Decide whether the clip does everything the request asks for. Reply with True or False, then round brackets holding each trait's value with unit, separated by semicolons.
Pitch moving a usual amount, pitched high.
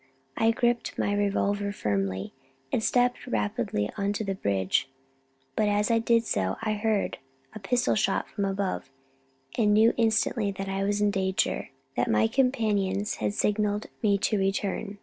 False (2.0 semitones; 205 Hz)